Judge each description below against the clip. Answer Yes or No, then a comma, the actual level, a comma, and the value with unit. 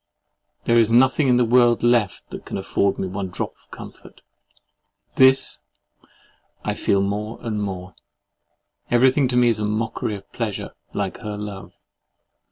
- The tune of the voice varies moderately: Yes, average, 3.3 semitones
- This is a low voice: Yes, low, 110 Hz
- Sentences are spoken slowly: No, average, 150 wpm